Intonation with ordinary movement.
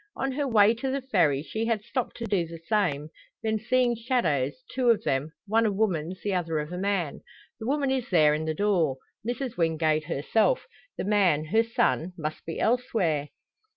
No: wide, 6.7 semitones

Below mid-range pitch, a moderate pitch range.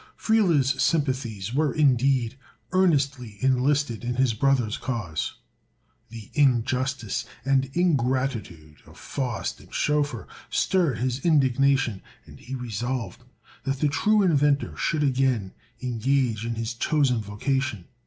Yes: low, 130 Hz; average, 3.3 semitones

